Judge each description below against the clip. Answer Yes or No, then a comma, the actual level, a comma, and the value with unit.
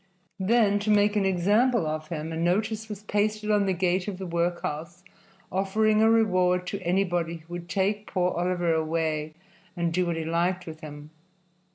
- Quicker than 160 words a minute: Yes, average, 180 wpm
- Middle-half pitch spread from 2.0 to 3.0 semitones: No, average, 3.5 semitones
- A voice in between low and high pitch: Yes, medium, 180 Hz